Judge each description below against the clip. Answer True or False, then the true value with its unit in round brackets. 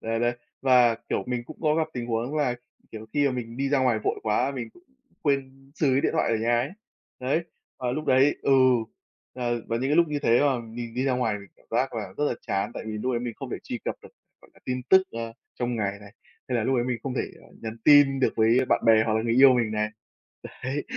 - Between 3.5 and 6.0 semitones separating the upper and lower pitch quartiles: False (2.9 semitones)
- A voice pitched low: True (125 Hz)